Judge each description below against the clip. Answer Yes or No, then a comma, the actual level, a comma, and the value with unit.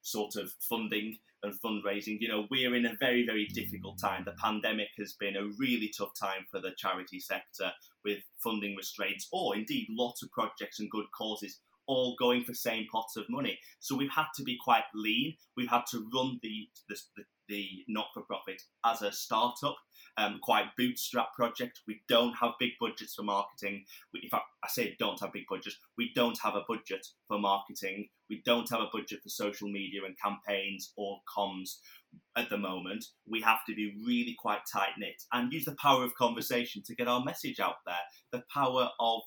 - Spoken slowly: No, average, 200 wpm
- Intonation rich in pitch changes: No, average, 3.3 semitones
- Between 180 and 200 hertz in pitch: No, low, 110 Hz